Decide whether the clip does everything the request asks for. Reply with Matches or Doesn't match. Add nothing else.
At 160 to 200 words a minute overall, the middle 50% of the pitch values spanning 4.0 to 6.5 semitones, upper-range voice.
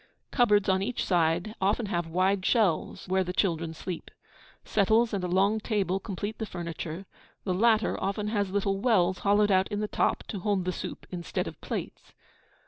Doesn't match